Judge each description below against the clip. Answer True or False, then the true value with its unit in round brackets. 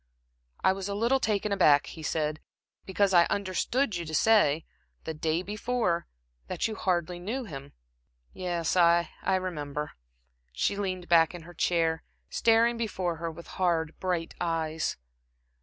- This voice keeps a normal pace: True (150 wpm)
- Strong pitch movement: False (3.7 semitones)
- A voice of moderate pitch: True (175 Hz)